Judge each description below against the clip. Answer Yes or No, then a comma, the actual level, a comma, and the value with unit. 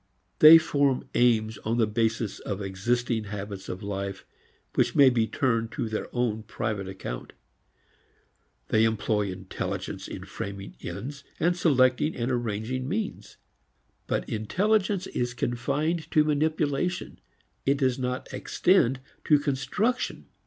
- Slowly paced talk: Yes, slow, 125 wpm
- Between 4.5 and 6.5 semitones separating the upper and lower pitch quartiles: Yes, average, 4.9 semitones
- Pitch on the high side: No, low, 120 Hz